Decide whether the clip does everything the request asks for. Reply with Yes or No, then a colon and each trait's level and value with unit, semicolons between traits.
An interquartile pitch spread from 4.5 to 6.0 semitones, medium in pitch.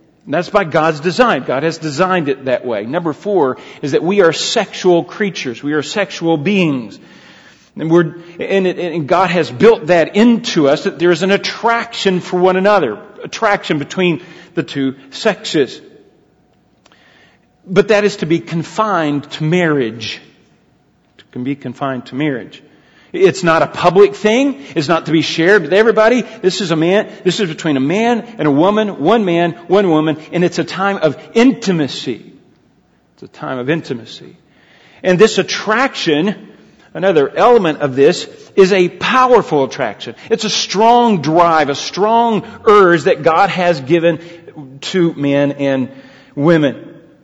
Yes: average, 4.8 semitones; medium, 175 Hz